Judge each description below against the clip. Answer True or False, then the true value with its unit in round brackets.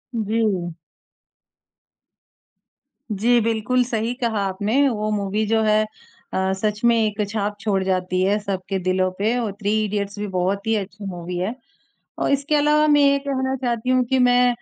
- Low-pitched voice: False (215 Hz)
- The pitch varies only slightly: False (3.7 semitones)